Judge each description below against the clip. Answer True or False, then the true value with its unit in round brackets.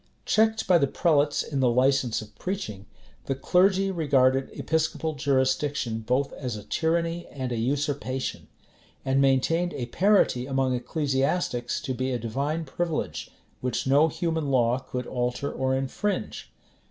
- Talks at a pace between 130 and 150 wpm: True (140 wpm)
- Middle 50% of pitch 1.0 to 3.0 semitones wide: False (4.0 semitones)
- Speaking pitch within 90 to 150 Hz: True (135 Hz)